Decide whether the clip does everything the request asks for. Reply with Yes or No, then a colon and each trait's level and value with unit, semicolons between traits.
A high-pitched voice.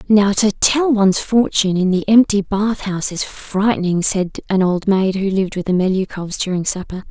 Yes: high, 195 Hz